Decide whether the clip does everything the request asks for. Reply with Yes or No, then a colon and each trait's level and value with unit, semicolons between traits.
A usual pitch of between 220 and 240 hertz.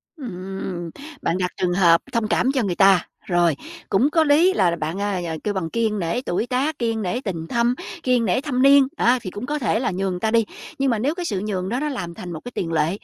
No: high, 210 Hz